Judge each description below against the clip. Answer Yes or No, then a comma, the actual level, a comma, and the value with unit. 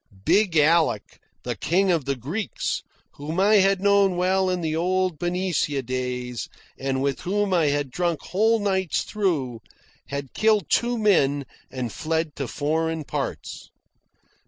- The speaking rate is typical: Yes, average, 145 wpm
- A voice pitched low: No, medium, 165 Hz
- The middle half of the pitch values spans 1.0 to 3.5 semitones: No, average, 5.3 semitones